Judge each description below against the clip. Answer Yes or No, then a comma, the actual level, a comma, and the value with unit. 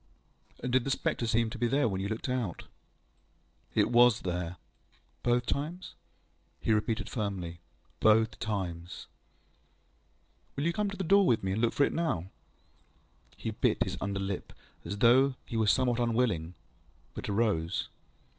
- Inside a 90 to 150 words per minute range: No, average, 160 wpm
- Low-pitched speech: Yes, low, 115 Hz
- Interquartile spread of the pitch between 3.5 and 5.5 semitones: Yes, average, 4.6 semitones